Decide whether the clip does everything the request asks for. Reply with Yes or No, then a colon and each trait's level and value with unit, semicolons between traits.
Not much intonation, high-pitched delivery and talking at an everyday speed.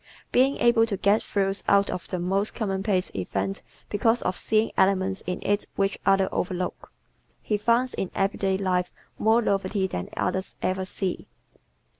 Yes: narrow, 2.1 semitones; high, 195 Hz; average, 155 wpm